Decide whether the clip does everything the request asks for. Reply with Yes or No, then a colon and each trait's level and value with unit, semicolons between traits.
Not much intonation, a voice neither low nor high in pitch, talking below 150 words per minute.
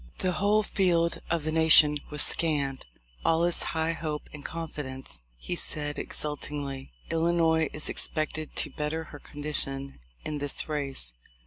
Yes: narrow, 2.1 semitones; medium, 155 Hz; average, 140 wpm